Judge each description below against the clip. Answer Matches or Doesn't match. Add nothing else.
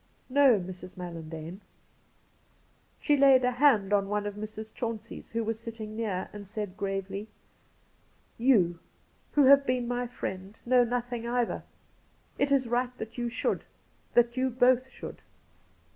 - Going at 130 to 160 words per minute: Matches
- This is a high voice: Matches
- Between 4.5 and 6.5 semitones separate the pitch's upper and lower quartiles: Doesn't match